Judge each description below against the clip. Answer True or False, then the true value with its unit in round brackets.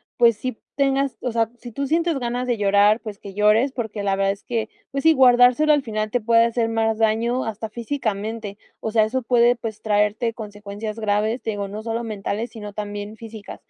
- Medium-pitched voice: False (225 Hz)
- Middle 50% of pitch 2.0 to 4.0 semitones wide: True (2.5 semitones)